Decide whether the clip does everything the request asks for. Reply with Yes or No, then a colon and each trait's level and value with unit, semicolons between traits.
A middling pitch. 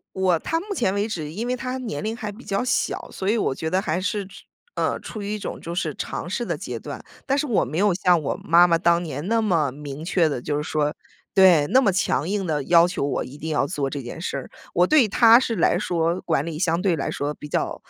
Yes: medium, 175 Hz